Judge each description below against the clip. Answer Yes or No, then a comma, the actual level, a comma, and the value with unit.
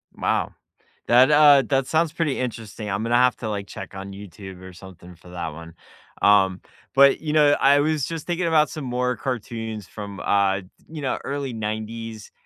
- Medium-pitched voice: No, low, 115 Hz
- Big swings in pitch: Yes, wide, 6.1 semitones